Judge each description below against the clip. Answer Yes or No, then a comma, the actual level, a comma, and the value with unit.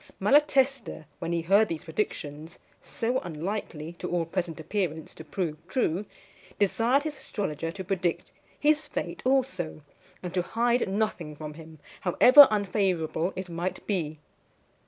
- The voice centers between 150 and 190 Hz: Yes, medium, 185 Hz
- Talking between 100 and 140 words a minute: Yes, slow, 135 wpm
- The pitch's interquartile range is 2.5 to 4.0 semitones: No, wide, 5.4 semitones